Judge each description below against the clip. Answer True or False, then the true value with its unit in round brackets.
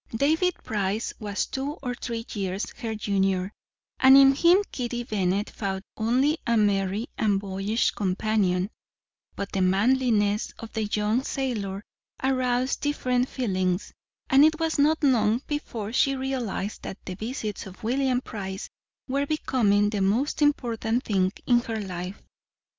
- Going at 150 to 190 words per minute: False (140 wpm)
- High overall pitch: True (225 Hz)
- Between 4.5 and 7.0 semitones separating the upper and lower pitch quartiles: True (4.8 semitones)